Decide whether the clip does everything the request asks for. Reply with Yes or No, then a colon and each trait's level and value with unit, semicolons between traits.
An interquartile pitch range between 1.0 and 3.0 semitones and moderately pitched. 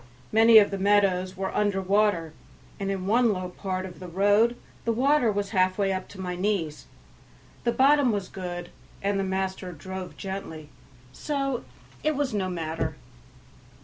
No: average, 2.7 semitones; high, 195 Hz